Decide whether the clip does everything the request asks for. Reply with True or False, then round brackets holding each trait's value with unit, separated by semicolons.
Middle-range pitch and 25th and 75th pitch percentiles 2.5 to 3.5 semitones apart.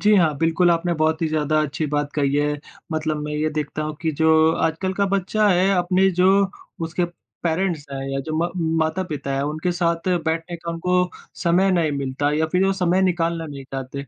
True (160 Hz; 2.9 semitones)